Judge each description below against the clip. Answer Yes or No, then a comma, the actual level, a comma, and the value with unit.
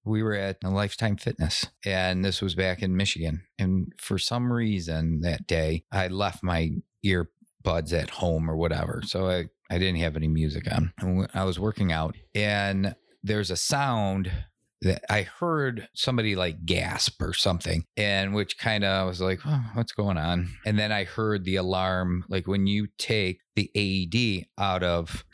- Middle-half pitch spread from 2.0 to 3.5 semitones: Yes, average, 2.8 semitones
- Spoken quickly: No, average, 180 wpm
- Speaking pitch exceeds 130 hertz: No, very low, 95 Hz